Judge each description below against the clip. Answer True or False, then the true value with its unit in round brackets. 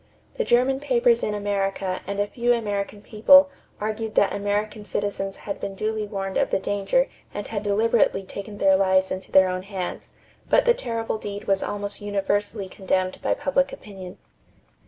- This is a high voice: True (205 Hz)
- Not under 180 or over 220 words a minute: False (170 wpm)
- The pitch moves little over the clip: True (2.3 semitones)